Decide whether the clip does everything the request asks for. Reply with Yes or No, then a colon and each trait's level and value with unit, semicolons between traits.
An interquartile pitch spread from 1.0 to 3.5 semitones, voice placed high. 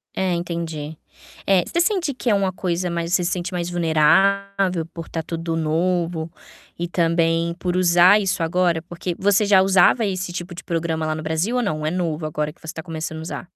No: narrow, 2.4 semitones; medium, 175 Hz